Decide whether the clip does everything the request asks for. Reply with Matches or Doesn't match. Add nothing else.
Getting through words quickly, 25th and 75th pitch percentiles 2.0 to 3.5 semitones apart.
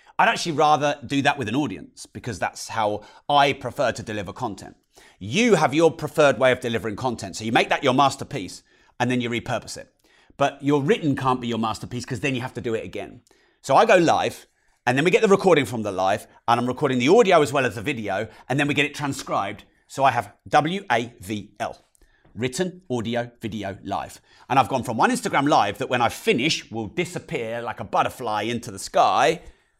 Doesn't match